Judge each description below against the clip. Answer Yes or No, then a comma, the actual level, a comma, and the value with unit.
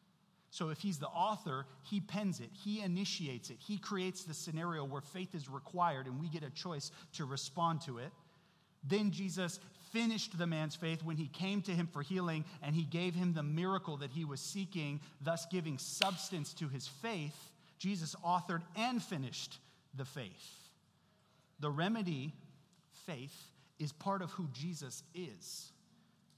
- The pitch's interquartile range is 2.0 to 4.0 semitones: Yes, average, 3.5 semitones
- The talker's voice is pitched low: No, medium, 170 Hz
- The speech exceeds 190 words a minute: No, average, 165 wpm